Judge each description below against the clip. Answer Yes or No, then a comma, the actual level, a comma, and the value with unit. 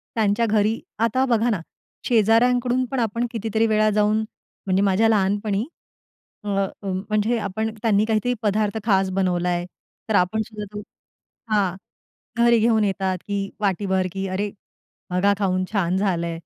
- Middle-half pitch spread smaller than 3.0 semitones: Yes, narrow, 2.5 semitones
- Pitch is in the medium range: No, high, 210 Hz